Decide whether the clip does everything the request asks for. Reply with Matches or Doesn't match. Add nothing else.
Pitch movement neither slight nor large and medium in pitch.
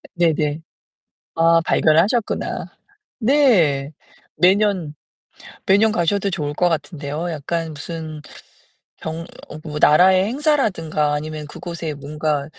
Matches